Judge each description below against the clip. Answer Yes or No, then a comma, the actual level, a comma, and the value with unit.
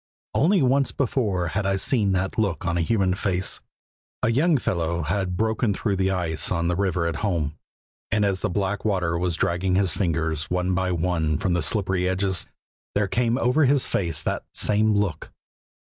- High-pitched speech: No, very low, 95 Hz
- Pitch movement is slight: No, average, 3.4 semitones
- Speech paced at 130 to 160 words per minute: No, average, 185 wpm